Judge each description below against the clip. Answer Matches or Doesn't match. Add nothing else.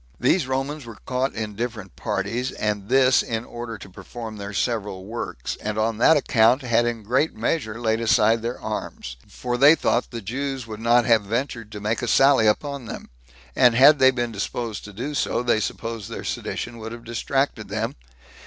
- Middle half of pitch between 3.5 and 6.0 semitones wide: Doesn't match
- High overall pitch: Doesn't match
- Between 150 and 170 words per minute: Doesn't match